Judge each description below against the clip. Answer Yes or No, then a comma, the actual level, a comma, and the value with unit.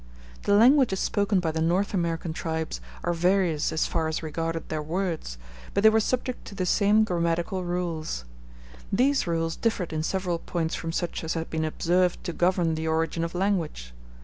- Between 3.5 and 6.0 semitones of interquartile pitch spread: No, average, 3.1 semitones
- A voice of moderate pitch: Yes, medium, 170 Hz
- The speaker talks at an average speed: Yes, average, 180 wpm